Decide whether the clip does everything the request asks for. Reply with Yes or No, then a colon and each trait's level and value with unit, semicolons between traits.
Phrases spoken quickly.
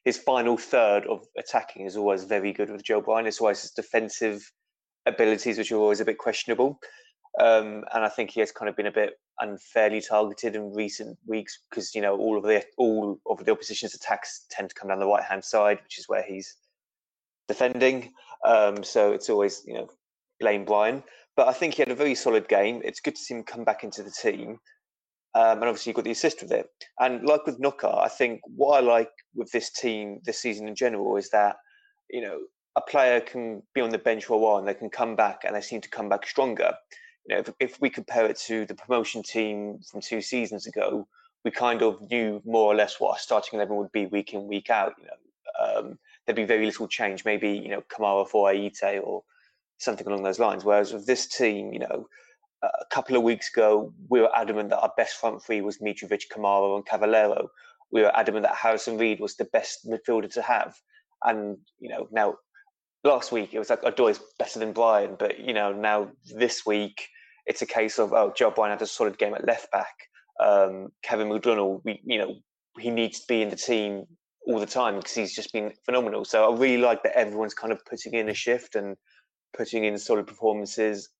Yes: fast, 220 wpm